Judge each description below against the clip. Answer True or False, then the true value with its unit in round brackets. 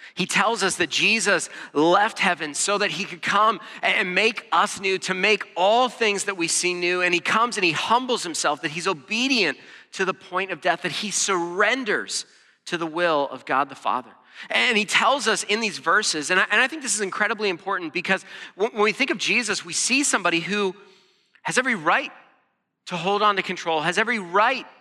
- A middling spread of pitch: True (3.4 semitones)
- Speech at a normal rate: False (210 wpm)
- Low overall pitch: False (195 Hz)